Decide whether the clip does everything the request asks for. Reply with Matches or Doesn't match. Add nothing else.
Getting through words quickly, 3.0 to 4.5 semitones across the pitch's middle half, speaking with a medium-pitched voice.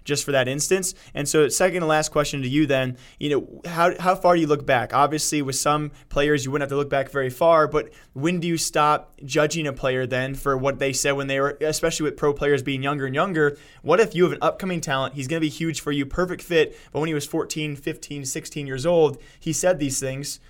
Doesn't match